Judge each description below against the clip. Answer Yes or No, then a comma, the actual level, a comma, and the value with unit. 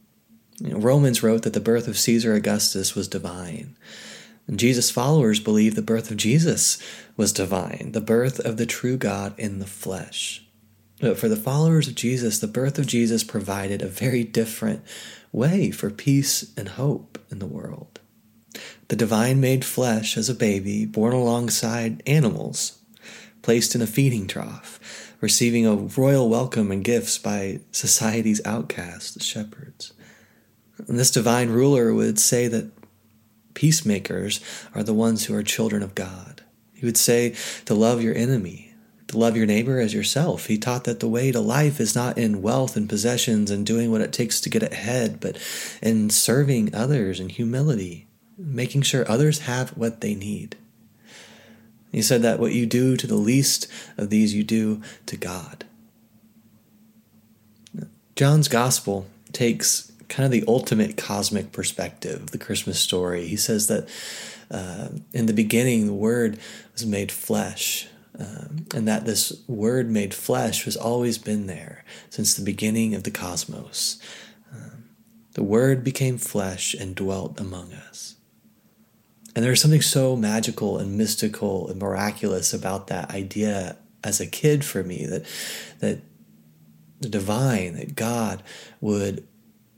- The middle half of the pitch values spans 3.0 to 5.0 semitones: No, narrow, 2.6 semitones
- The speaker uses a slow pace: No, average, 155 wpm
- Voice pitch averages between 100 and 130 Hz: Yes, low, 115 Hz